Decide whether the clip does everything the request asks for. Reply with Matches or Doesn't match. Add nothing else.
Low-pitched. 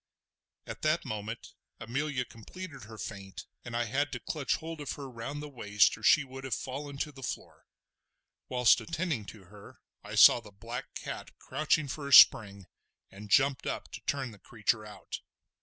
Matches